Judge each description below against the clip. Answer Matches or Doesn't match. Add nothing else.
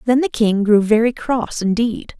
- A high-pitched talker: Matches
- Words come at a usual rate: Matches